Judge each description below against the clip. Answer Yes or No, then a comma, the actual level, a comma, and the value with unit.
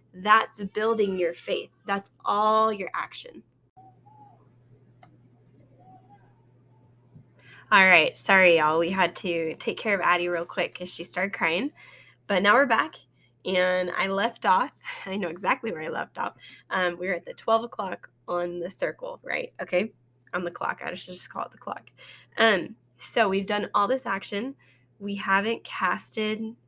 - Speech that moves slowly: No, average, 160 wpm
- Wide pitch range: Yes, wide, 8.0 semitones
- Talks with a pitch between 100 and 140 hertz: No, medium, 180 Hz